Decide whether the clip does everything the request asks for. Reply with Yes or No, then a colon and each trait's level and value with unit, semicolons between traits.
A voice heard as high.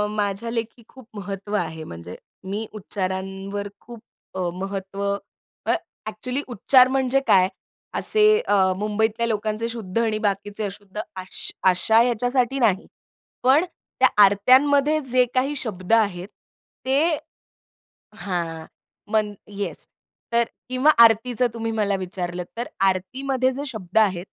Yes: high, 215 Hz